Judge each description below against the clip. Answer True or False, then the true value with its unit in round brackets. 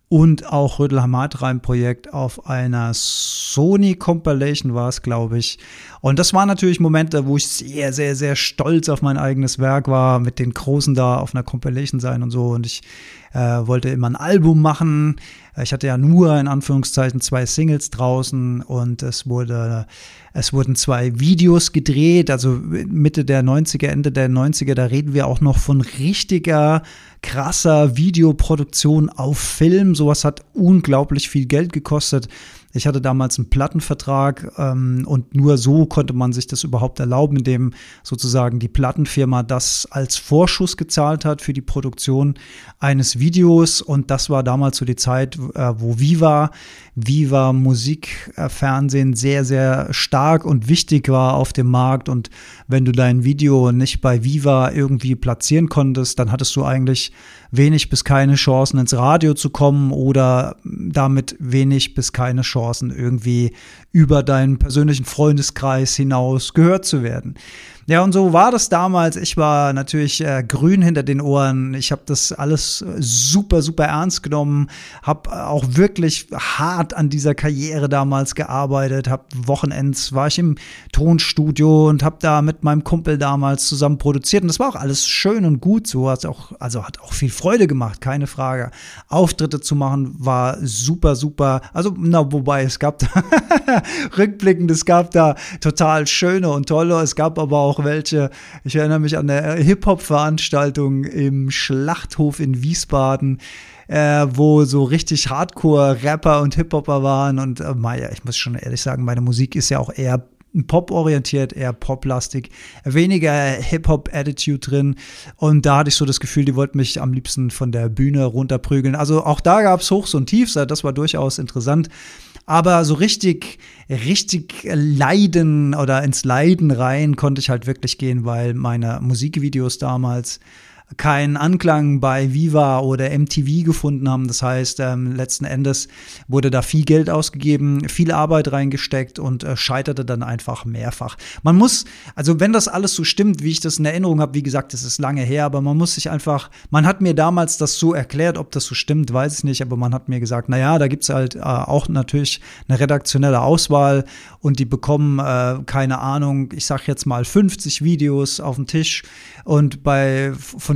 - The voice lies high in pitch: False (140 Hz)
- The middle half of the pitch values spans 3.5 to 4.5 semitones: False (2.9 semitones)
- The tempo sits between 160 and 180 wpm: True (170 wpm)